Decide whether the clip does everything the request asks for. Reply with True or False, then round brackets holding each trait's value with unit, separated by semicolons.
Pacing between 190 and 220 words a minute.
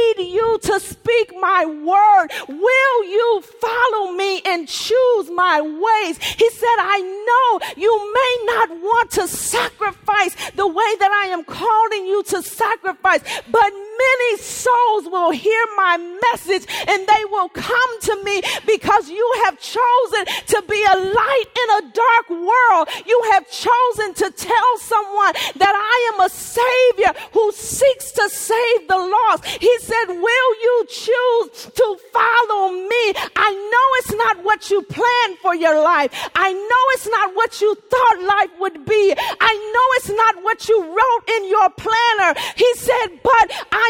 False (160 wpm)